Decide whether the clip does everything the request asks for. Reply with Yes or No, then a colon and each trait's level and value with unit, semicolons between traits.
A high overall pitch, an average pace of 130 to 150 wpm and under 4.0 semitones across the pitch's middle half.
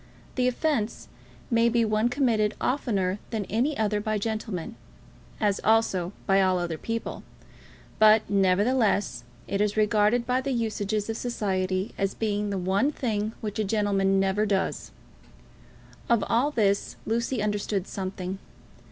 Yes: high, 210 Hz; average, 140 wpm; average, 2.7 semitones